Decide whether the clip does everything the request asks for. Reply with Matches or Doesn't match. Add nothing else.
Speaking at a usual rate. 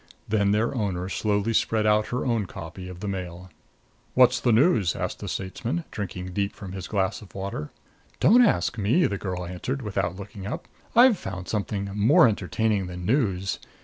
Matches